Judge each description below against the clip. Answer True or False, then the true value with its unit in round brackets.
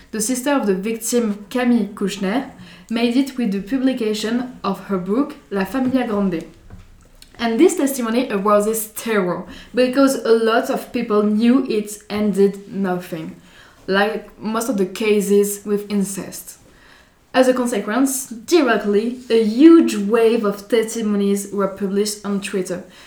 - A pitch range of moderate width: True (3.4 semitones)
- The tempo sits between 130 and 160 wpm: True (135 wpm)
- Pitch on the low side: False (215 Hz)